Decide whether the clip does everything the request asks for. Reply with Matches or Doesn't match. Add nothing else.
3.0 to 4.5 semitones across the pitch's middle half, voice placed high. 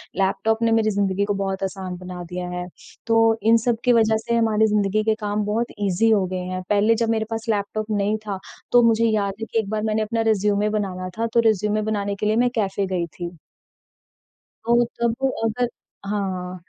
Doesn't match